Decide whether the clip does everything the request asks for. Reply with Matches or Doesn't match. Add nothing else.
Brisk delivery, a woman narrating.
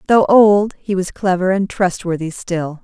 Doesn't match